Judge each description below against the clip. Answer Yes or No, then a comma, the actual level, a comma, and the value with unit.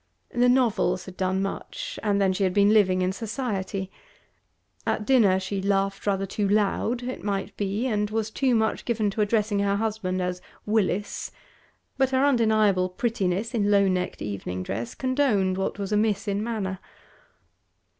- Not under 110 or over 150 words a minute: No, average, 165 wpm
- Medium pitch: No, high, 205 Hz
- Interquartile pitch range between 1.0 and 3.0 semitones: Yes, average, 2.7 semitones